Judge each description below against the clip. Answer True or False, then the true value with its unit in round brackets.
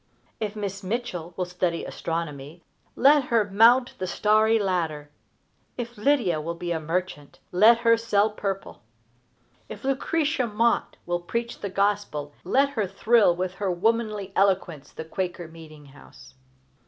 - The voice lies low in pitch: False (195 Hz)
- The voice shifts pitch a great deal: False (5.0 semitones)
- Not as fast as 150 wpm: True (140 wpm)